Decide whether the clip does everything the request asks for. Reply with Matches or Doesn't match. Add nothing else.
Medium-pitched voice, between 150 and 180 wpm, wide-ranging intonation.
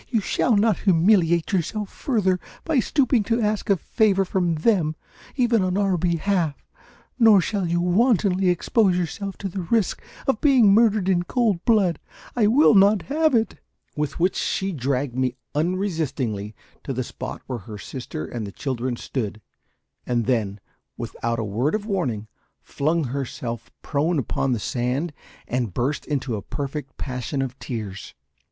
Matches